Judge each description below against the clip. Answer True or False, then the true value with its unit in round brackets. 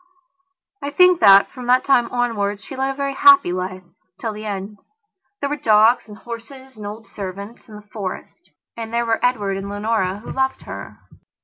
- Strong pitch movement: False (3.9 semitones)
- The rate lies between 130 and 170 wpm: False (190 wpm)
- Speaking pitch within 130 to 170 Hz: False (225 Hz)